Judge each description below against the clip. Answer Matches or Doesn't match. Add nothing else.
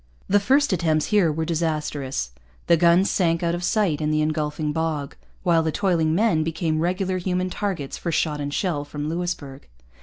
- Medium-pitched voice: Matches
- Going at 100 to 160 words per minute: Doesn't match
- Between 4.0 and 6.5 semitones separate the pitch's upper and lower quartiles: Doesn't match